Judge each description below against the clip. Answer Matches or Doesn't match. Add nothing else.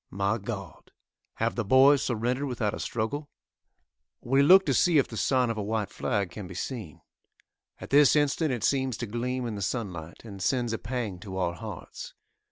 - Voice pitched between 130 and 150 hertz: Doesn't match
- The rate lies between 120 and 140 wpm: Doesn't match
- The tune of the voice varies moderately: Matches